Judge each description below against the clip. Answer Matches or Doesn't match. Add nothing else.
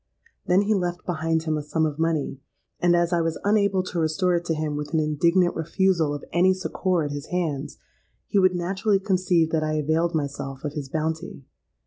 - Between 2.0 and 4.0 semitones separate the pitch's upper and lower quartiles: Matches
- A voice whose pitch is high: Doesn't match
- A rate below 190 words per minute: Doesn't match